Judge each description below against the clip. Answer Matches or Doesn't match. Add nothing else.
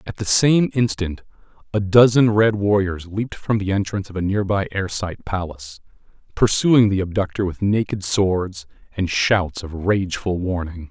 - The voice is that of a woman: Doesn't match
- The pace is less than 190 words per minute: Matches